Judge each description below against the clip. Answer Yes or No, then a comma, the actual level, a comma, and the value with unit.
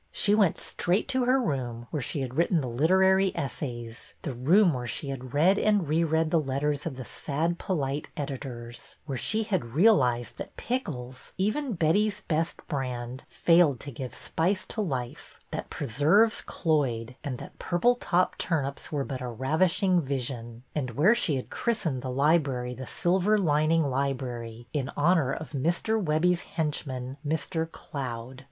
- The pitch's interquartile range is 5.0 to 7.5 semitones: Yes, wide, 5.5 semitones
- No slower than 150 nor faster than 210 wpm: Yes, average, 165 wpm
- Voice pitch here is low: No, medium, 150 Hz